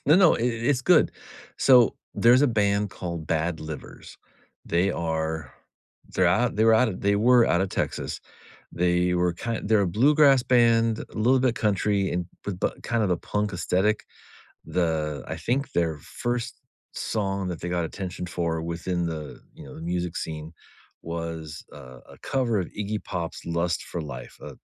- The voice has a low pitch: Yes, very low, 95 Hz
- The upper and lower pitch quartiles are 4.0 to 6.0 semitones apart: Yes, average, 5.3 semitones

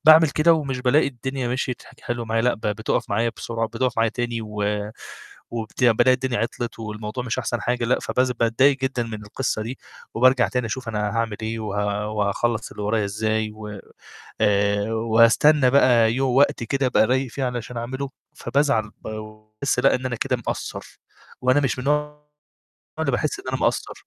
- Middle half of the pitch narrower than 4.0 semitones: Yes, average, 2.8 semitones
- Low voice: Yes, low, 120 Hz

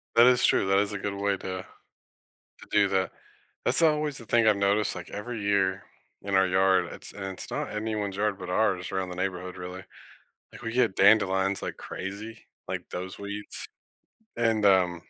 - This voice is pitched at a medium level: No, low, 100 Hz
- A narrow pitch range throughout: Yes, narrow, 2.3 semitones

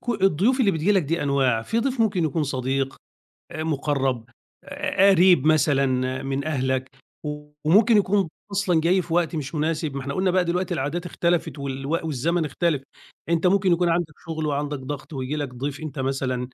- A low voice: No, medium, 155 Hz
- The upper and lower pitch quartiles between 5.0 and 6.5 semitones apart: No, average, 4.5 semitones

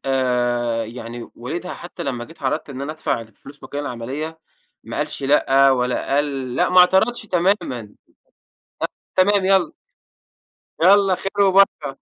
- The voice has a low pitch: No, medium, 145 Hz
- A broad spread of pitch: Yes, wide, 6.5 semitones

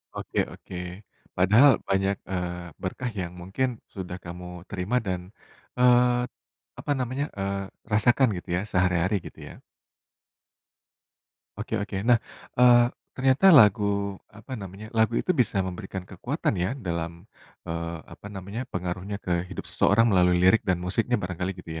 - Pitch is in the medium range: No, very low, 95 Hz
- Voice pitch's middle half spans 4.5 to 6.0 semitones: Yes, average, 4.8 semitones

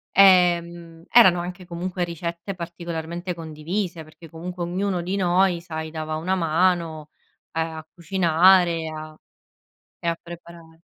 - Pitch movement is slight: Yes, narrow, 1.8 semitones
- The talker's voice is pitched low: No, medium, 170 Hz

